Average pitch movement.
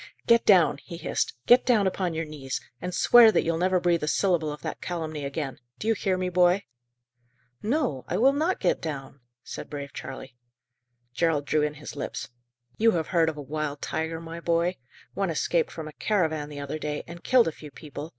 Yes: average, 3.6 semitones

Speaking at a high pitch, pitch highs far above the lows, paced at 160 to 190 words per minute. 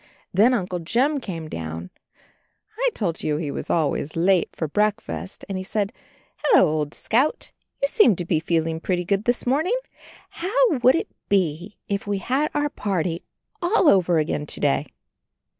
Yes: high, 195 Hz; wide, 7.5 semitones; average, 165 wpm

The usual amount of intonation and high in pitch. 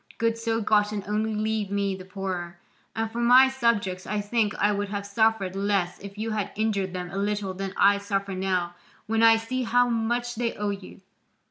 No: narrow, 2.3 semitones; high, 205 Hz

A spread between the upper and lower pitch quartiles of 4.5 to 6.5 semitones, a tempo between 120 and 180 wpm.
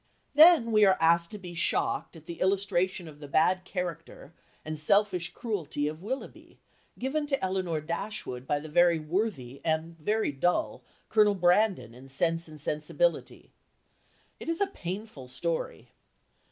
Yes: average, 5.0 semitones; average, 150 wpm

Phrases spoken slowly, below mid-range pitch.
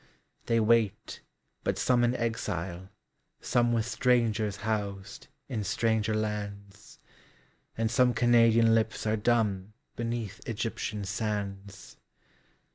Yes: slow, 90 wpm; low, 110 Hz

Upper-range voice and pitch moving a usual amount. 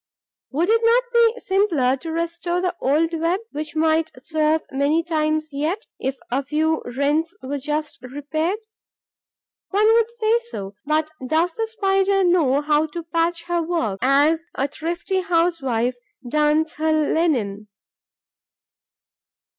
Yes: very high, 315 Hz; average, 3.2 semitones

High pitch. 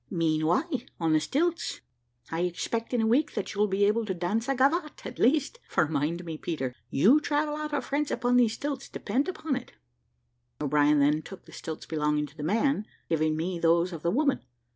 Yes: high, 195 Hz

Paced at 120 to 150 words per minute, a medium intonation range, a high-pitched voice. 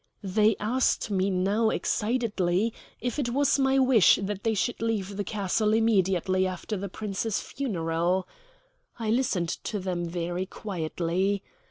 Yes: average, 140 wpm; average, 3.5 semitones; high, 200 Hz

